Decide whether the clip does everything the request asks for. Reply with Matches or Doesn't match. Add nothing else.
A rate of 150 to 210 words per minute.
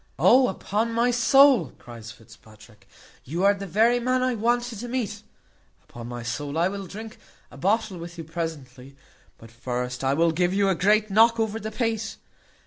Matches